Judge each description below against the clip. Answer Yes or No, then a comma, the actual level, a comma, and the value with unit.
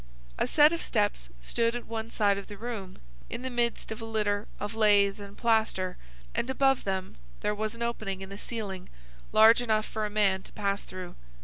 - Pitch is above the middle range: Yes, high, 215 Hz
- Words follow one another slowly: No, fast, 205 wpm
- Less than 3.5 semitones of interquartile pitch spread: Yes, narrow, 2.6 semitones